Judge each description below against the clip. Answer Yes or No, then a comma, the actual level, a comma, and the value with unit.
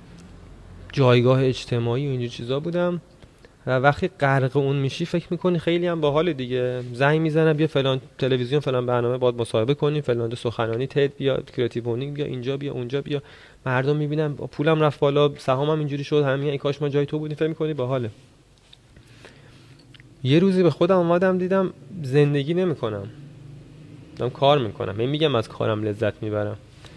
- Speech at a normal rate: No, fast, 160 wpm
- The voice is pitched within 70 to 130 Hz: No, medium, 140 Hz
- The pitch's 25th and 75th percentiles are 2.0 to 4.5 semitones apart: Yes, average, 3.3 semitones